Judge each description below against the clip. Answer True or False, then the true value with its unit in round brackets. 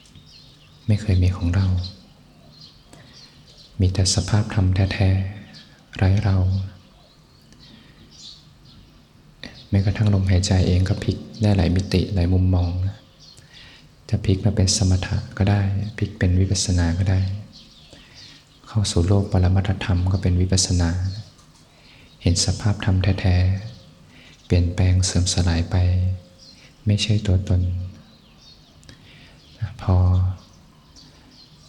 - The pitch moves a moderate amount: False (2.0 semitones)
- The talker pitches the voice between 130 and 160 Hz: False (95 Hz)